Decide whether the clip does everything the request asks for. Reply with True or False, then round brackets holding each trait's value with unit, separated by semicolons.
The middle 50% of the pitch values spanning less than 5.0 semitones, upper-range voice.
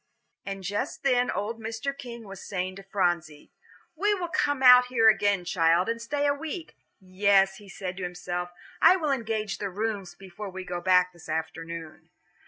False (5.4 semitones; 200 Hz)